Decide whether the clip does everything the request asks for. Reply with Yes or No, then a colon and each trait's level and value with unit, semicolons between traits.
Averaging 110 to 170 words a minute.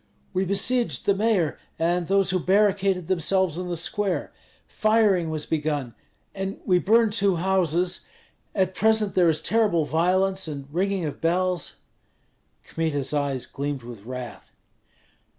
Yes: average, 140 wpm